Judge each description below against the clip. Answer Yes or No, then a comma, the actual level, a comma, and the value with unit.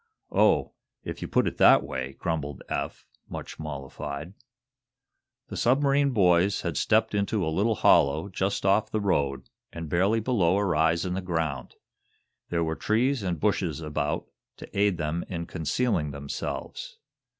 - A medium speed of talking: Yes, average, 150 wpm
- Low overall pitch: Yes, very low, 85 Hz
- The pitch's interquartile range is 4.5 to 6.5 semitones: Yes, average, 5.0 semitones